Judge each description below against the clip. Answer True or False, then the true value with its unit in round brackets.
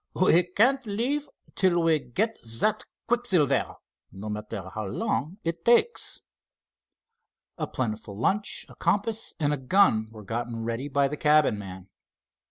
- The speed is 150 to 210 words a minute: False (140 wpm)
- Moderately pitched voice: True (150 Hz)